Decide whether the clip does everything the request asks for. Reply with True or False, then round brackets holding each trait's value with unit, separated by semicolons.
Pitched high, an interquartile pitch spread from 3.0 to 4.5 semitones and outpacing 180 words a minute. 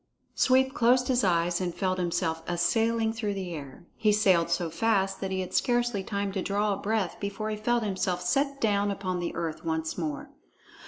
True (195 Hz; 4.0 semitones; 200 wpm)